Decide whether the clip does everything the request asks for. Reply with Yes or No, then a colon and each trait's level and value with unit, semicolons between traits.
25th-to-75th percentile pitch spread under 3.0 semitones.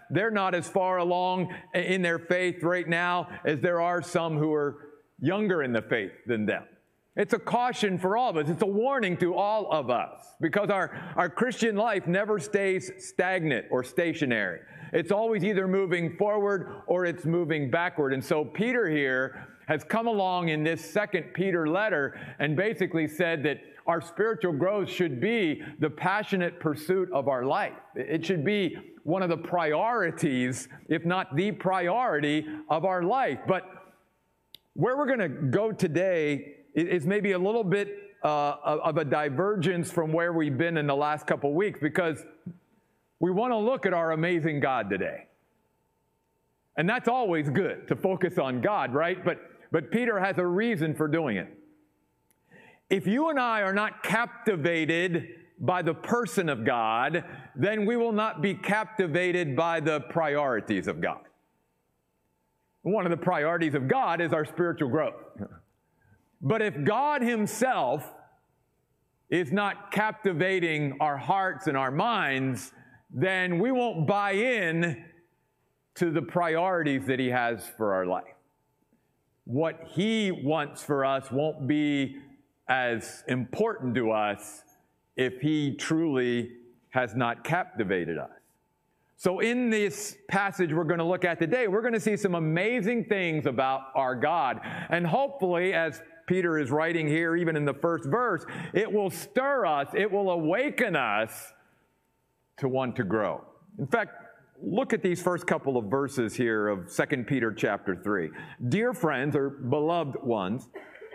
No: average, 4.5 semitones